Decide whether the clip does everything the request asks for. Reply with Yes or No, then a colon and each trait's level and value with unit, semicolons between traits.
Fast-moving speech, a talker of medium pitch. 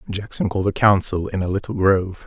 No: fast, 210 wpm; very low, 95 Hz